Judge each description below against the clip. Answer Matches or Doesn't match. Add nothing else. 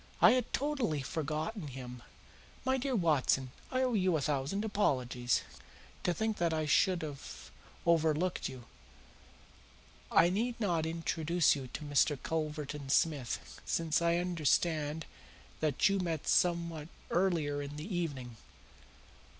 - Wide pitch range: Doesn't match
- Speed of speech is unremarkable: Doesn't match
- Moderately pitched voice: Matches